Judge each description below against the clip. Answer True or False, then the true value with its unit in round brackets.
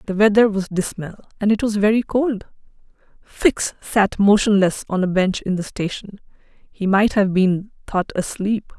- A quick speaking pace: False (165 wpm)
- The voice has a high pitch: True (200 Hz)